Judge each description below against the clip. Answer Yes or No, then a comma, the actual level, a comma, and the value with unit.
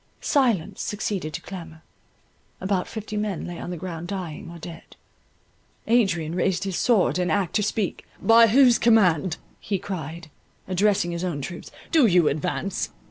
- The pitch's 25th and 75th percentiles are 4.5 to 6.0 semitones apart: No, average, 3.5 semitones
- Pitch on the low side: No, medium, 185 Hz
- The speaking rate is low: No, average, 155 wpm